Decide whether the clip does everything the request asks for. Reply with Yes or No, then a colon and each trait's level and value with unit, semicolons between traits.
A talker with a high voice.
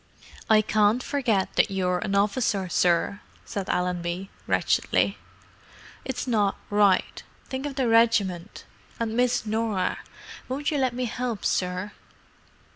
Yes: high, 210 Hz